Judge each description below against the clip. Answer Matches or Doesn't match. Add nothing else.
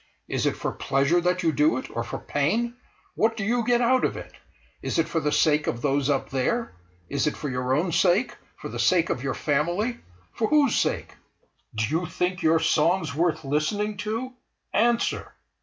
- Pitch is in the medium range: Matches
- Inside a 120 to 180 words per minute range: Doesn't match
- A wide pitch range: Matches